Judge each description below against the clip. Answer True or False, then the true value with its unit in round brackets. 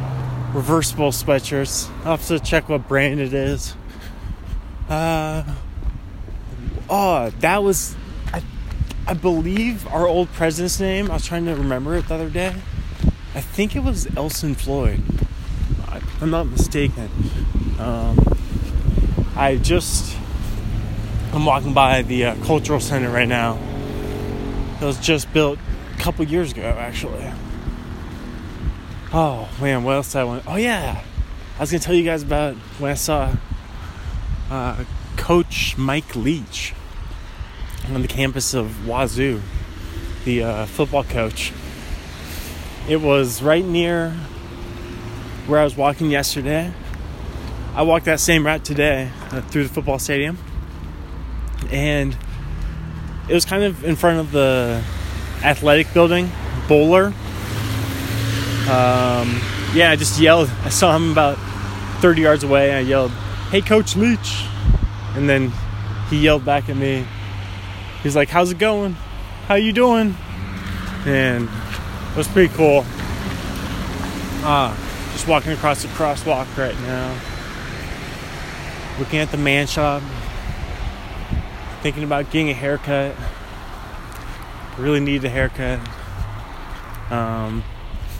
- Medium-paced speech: False (125 wpm)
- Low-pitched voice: True (125 Hz)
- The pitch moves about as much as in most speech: False (7.6 semitones)